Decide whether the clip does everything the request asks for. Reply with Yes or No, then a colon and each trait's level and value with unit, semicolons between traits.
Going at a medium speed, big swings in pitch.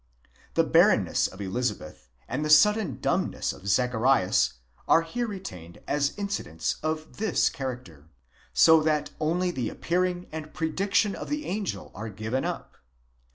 Yes: average, 150 wpm; wide, 8.2 semitones